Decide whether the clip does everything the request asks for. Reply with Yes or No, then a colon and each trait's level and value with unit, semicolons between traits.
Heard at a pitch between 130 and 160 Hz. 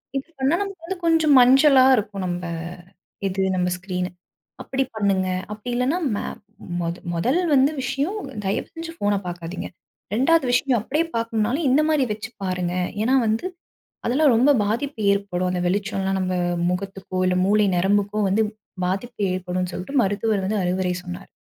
No: high, 210 Hz